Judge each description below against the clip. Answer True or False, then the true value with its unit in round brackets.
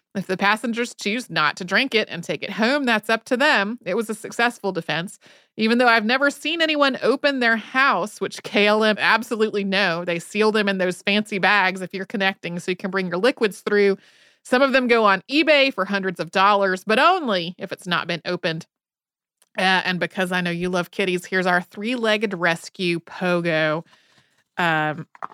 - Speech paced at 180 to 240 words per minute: True (195 wpm)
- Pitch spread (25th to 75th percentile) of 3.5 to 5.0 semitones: True (4.2 semitones)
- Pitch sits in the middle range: False (200 Hz)